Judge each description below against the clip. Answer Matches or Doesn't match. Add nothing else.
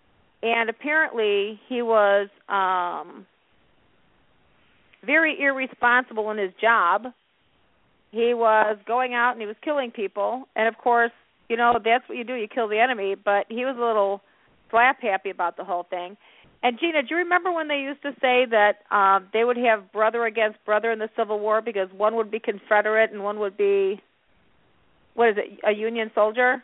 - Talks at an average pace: Matches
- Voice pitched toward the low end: Doesn't match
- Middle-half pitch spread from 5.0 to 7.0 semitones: Doesn't match